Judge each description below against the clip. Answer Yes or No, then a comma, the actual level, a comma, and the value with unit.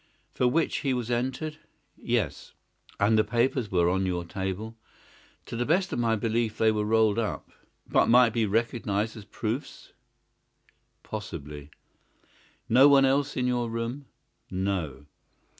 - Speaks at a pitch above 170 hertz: No, low, 115 Hz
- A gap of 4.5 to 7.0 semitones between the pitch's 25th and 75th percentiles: No, average, 3.7 semitones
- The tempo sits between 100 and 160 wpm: Yes, average, 140 wpm